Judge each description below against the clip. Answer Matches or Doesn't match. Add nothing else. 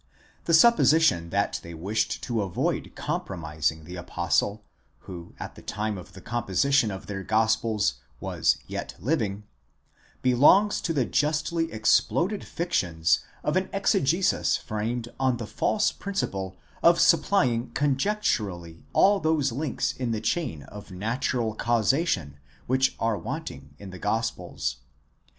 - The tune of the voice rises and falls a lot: Matches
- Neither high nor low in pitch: Doesn't match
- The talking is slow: Matches